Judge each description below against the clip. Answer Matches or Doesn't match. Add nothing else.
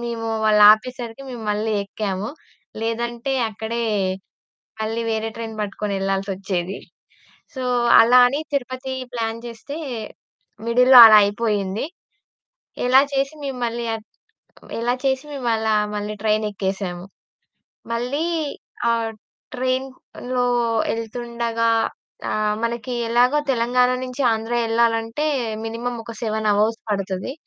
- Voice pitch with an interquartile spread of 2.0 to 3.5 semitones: Matches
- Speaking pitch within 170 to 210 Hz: Doesn't match